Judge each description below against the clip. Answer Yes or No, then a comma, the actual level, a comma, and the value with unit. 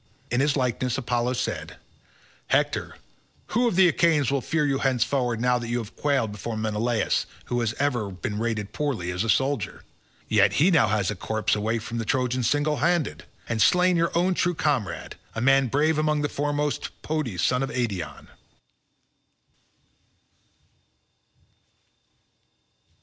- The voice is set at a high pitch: No, low, 125 Hz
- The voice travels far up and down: No, average, 4.8 semitones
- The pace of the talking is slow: No, average, 155 wpm